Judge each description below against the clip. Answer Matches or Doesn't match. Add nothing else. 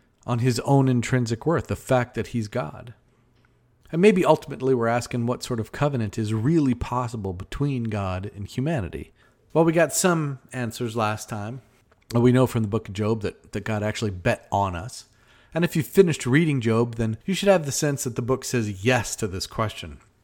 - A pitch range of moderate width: Matches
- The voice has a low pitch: Matches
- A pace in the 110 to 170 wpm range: Doesn't match